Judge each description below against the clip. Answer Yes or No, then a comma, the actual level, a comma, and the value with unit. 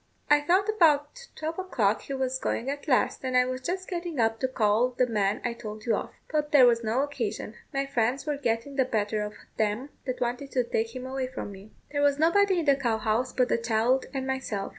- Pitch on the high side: Yes, very high, 255 Hz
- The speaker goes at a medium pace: No, fast, 235 wpm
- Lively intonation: No, average, 4.1 semitones